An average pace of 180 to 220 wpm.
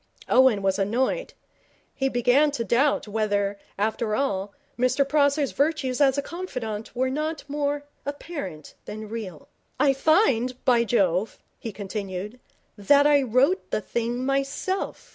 No: slow, 135 wpm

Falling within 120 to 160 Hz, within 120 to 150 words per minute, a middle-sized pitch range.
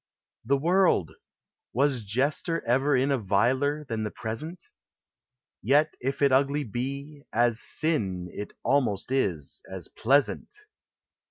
Yes: low, 135 Hz; average, 140 wpm; average, 4.3 semitones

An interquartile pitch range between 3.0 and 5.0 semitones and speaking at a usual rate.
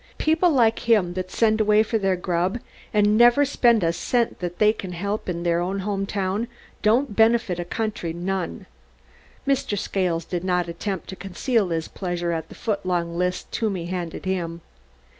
Yes: average, 3.7 semitones; average, 170 wpm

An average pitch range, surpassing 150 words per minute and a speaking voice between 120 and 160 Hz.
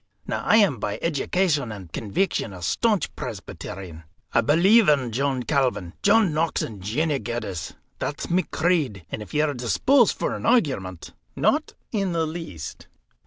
No: wide, 8.9 semitones; average, 165 wpm; medium, 140 Hz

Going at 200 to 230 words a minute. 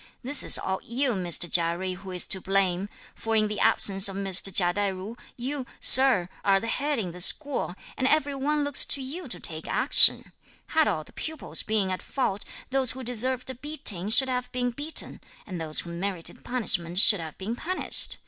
Yes: fast, 205 wpm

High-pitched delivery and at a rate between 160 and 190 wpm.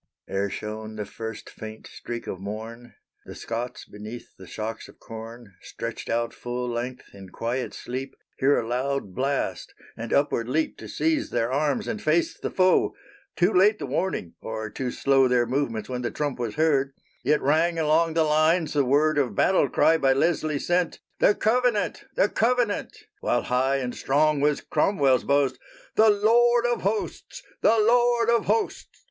No: medium, 140 Hz; average, 170 wpm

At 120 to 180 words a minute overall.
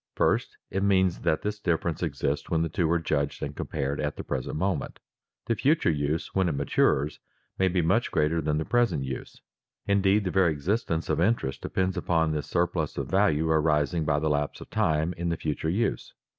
No: average, 200 wpm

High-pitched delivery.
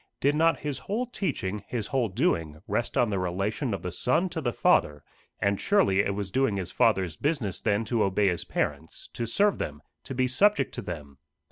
No: low, 105 Hz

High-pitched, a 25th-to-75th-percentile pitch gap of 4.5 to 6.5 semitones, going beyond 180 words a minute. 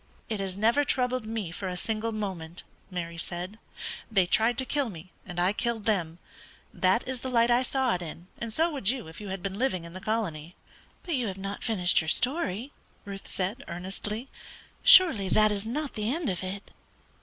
Yes: high, 210 Hz; average, 4.9 semitones; average, 200 wpm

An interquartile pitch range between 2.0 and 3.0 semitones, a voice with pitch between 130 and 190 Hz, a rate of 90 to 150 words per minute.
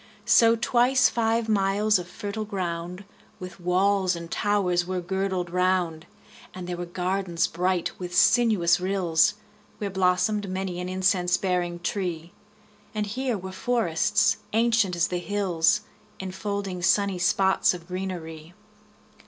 Yes: narrow, 2.4 semitones; medium, 185 Hz; slow, 135 wpm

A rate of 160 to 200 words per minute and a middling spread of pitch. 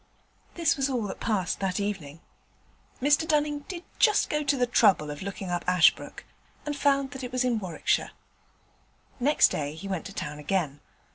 No: average, 180 wpm; wide, 8.0 semitones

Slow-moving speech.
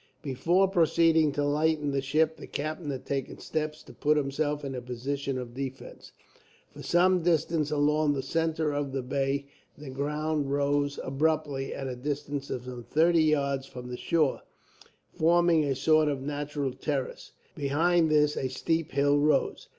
No: average, 165 wpm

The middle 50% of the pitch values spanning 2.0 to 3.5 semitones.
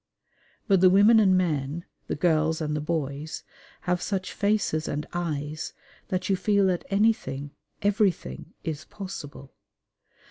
No: average, 4.6 semitones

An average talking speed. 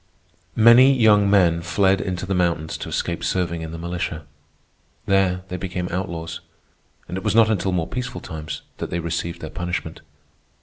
Yes: average, 170 wpm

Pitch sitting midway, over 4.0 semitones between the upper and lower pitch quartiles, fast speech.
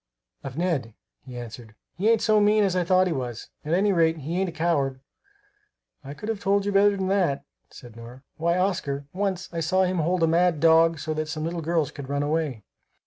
Yes: medium, 165 Hz; average, 4.6 semitones; fast, 220 wpm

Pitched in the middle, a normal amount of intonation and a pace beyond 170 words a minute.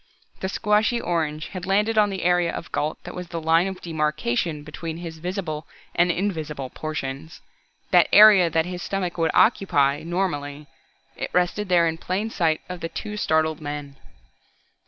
No: medium, 170 Hz; average, 3.4 semitones; average, 165 wpm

